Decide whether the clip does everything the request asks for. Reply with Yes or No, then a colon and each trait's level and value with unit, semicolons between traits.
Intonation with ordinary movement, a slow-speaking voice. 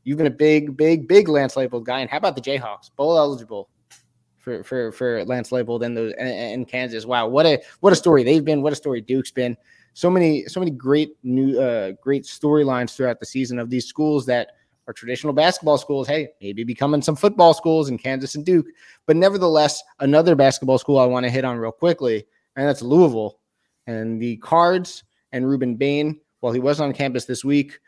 No: average, 3.5 semitones; fast, 205 wpm